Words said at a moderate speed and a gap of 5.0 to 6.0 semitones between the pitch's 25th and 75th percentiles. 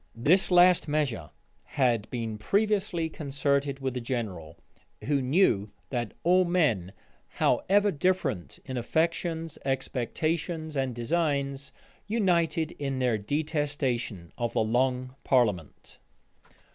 No: slow, 105 wpm; wide, 5.5 semitones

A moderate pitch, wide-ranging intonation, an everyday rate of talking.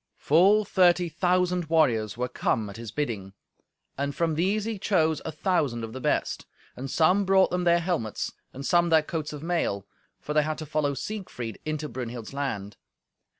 Yes: medium, 155 Hz; wide, 6.0 semitones; average, 180 wpm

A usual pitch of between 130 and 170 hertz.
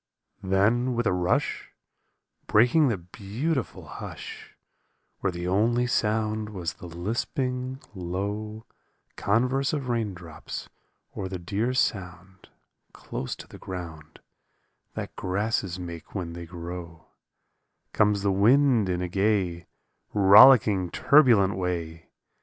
No: low, 100 Hz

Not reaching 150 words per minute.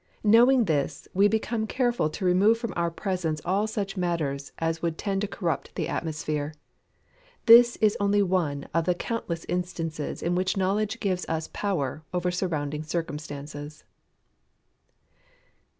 Yes: average, 140 wpm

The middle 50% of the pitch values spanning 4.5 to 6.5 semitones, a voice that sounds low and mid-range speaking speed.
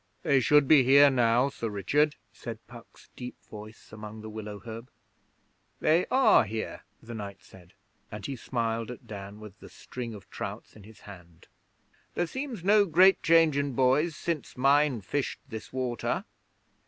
Yes: average, 5.1 semitones; low, 120 Hz; average, 165 wpm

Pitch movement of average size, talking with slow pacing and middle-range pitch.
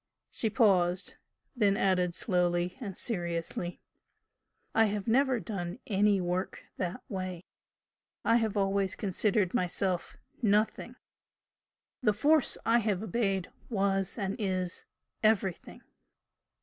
No: average, 3.3 semitones; slow, 110 wpm; high, 195 Hz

